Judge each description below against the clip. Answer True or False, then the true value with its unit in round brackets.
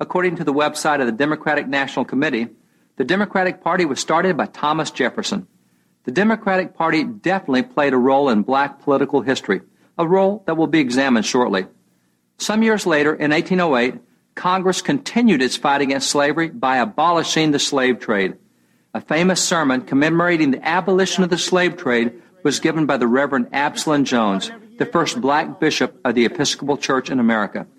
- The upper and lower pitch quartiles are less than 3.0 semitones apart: False (5.2 semitones)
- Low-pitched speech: False (155 Hz)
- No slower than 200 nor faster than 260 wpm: False (170 wpm)